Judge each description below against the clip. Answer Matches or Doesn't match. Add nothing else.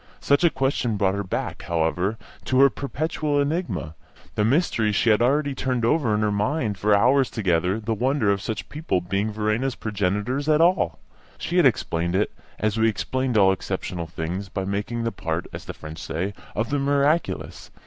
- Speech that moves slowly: Doesn't match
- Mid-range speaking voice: Doesn't match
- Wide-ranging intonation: Matches